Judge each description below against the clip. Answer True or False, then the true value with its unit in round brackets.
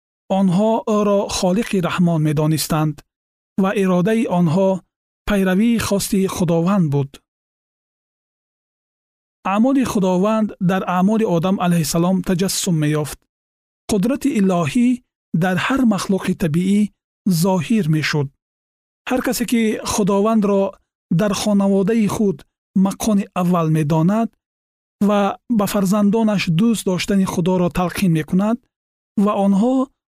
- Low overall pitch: False (195 Hz)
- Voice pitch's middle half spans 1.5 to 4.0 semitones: True (3.3 semitones)